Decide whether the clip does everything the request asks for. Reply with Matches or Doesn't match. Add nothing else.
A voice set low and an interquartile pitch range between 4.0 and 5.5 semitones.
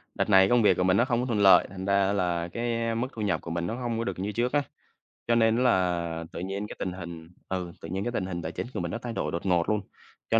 Matches